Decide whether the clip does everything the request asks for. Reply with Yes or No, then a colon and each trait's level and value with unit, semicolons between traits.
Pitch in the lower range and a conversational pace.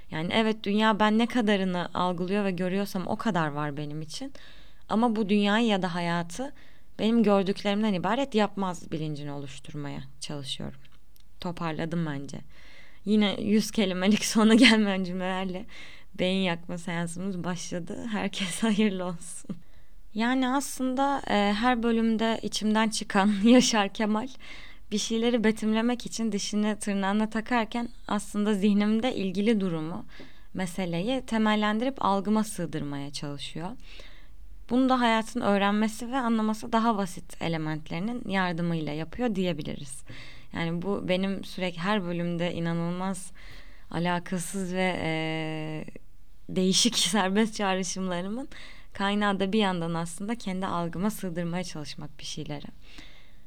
No: high, 195 Hz; average, 115 wpm